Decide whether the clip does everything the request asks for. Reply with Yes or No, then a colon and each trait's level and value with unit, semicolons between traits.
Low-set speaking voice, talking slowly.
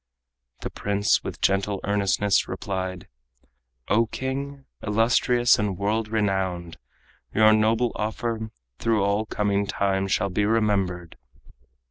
Yes: low, 105 Hz; slow, 110 wpm